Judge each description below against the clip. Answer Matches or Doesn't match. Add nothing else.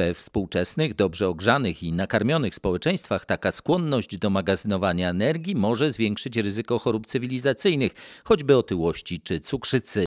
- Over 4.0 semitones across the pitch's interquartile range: Matches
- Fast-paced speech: Doesn't match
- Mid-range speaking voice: Doesn't match